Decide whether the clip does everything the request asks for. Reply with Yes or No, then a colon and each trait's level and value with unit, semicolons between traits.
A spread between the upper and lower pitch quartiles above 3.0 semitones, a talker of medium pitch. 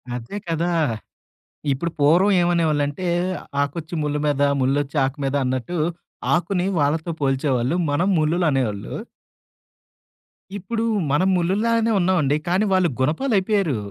Yes: average, 4.3 semitones; medium, 160 Hz